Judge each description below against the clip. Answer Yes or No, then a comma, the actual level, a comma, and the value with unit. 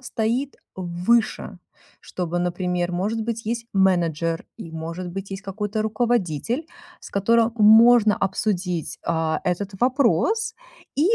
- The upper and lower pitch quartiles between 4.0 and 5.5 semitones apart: Yes, average, 4.7 semitones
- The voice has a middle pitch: No, high, 200 Hz